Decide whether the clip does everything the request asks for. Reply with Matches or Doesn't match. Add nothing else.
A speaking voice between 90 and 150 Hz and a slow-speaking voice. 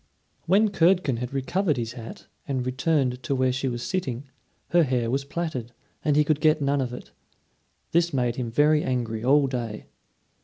Doesn't match